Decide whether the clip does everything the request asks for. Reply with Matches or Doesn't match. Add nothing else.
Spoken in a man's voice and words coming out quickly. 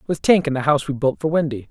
Matches